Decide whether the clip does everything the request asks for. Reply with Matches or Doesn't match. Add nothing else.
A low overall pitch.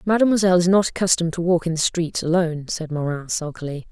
Doesn't match